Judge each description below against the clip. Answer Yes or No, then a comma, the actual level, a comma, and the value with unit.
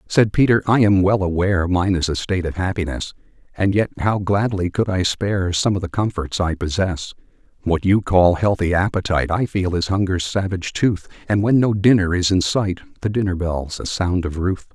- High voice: No, very low, 95 Hz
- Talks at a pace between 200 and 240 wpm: Yes, fast, 205 wpm